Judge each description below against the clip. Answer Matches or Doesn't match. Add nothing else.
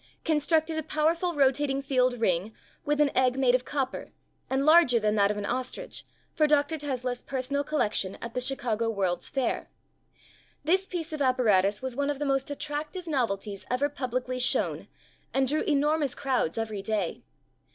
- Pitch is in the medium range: Doesn't match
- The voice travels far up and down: Doesn't match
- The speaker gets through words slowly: Doesn't match